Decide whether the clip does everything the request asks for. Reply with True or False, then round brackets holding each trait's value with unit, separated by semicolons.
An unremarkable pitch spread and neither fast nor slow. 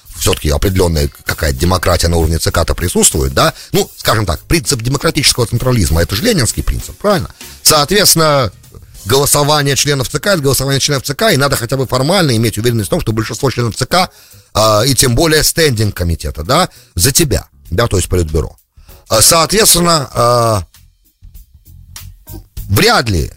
False (8.1 semitones; 150 wpm)